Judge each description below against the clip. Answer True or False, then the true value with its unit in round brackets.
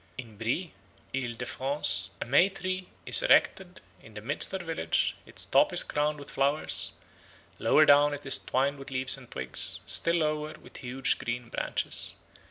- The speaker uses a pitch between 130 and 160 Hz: True (140 Hz)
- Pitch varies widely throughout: False (3.8 semitones)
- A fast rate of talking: False (180 wpm)